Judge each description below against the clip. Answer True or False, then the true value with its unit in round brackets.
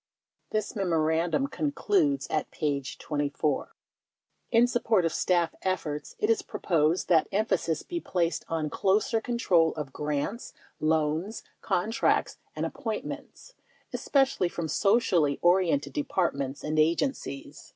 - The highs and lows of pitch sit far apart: True (6.5 semitones)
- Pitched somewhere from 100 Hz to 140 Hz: False (175 Hz)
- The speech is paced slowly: True (120 wpm)